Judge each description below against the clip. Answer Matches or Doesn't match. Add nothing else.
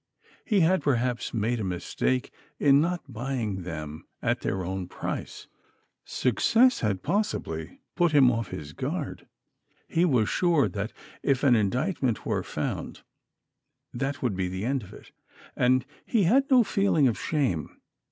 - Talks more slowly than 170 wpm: Matches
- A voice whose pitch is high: Doesn't match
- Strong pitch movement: Matches